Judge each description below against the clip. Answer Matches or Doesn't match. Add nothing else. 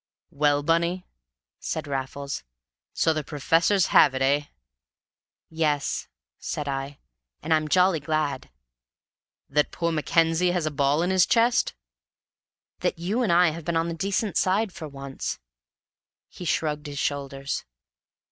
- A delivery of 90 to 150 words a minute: Matches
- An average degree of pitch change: Matches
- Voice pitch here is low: Doesn't match